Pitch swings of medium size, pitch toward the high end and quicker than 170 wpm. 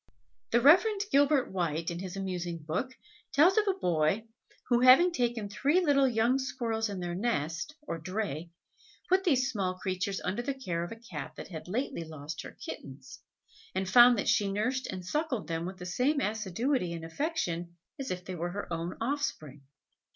No: wide, 7.2 semitones; high, 205 Hz; average, 180 wpm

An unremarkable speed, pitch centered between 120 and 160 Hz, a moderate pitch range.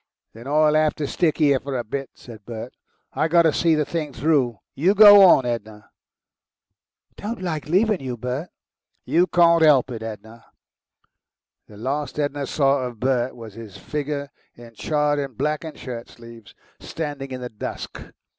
Yes: average, 165 wpm; medium, 140 Hz; average, 4.4 semitones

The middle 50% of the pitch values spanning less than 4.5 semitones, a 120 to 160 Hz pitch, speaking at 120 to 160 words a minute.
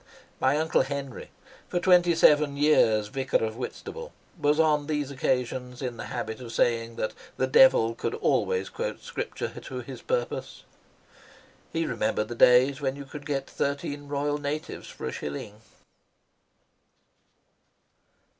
Yes: average, 3.7 semitones; medium, 140 Hz; average, 140 wpm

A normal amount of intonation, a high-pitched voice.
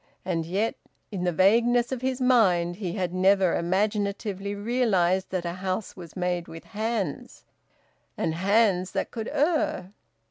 Yes: average, 3.7 semitones; high, 195 Hz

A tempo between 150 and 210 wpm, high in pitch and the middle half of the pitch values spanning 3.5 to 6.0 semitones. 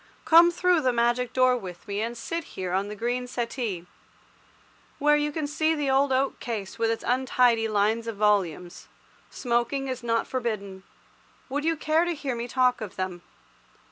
Yes: average, 175 wpm; high, 240 Hz; average, 4.4 semitones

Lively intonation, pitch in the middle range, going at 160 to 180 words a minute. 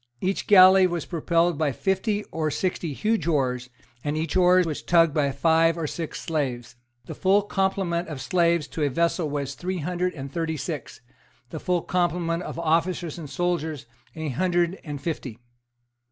No: average, 3.2 semitones; medium, 165 Hz; average, 170 wpm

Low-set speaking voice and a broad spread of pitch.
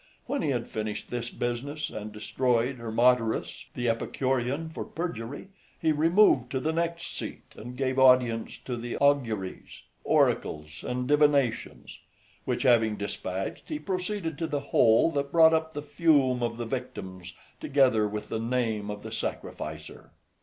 No: low, 125 Hz; average, 4.5 semitones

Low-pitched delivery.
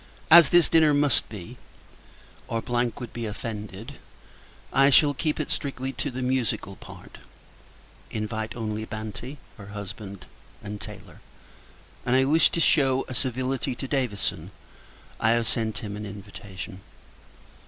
Yes: low, 120 Hz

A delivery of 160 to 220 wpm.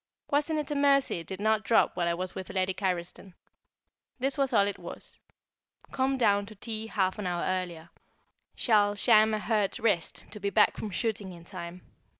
Yes: average, 190 wpm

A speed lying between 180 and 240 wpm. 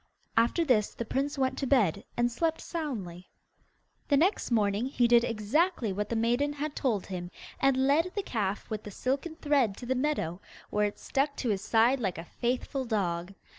Yes: average, 190 wpm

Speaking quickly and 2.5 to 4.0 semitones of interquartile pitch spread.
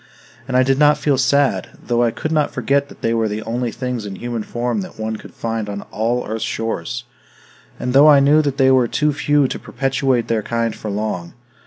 Yes: fast, 220 wpm; average, 3.5 semitones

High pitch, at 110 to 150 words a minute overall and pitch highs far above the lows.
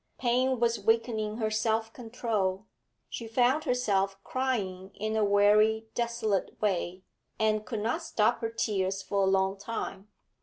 No: high, 220 Hz; average, 145 wpm; average, 2.8 semitones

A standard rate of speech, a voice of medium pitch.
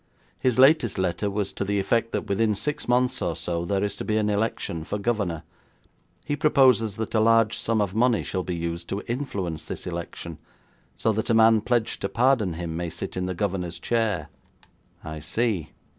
No: average, 195 wpm; low, 105 Hz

